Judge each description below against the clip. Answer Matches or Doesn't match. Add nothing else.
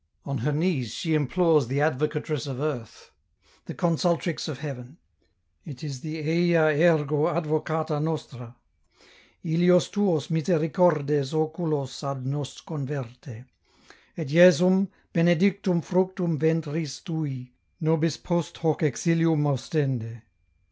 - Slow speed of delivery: Matches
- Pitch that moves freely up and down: Doesn't match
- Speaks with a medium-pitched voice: Matches